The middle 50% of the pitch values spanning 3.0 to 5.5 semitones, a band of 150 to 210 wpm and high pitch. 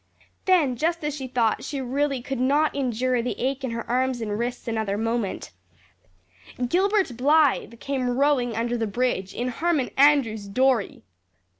Yes: average, 3.3 semitones; average, 155 wpm; very high, 255 Hz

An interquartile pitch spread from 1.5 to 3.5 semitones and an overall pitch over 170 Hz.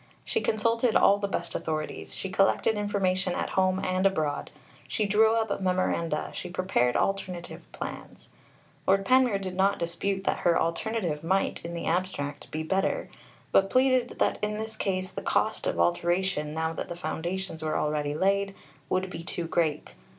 Yes: average, 3.2 semitones; medium, 185 Hz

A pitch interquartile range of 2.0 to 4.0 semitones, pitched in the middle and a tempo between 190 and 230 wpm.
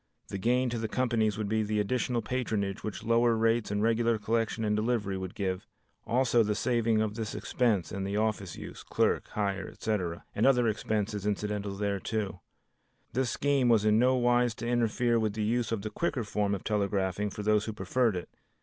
No: narrow, 2.5 semitones; low, 110 Hz; average, 195 wpm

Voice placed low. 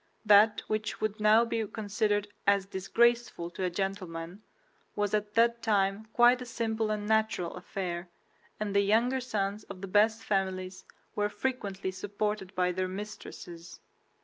No: high, 205 Hz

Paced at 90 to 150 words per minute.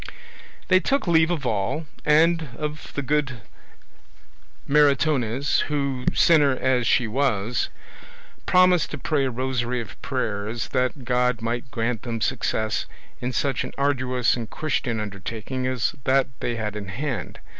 Yes: average, 140 wpm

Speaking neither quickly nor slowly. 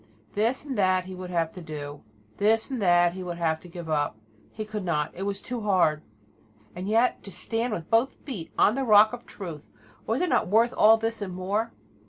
No: fast, 220 wpm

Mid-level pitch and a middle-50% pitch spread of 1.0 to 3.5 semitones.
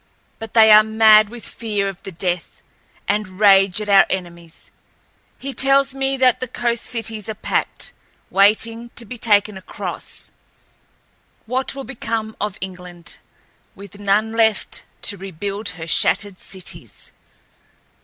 No: high, 210 Hz; average, 2.8 semitones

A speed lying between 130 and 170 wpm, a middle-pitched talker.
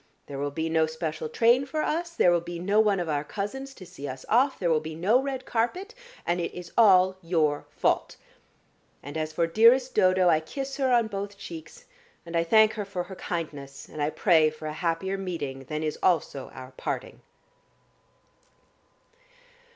No: average, 190 wpm; medium, 175 Hz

